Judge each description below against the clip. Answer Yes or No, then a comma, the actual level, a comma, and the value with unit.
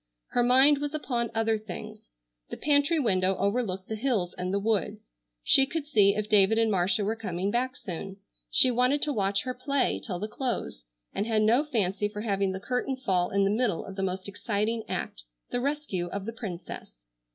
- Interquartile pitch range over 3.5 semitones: Yes, average, 4.3 semitones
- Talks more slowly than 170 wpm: No, average, 195 wpm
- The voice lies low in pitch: No, high, 215 Hz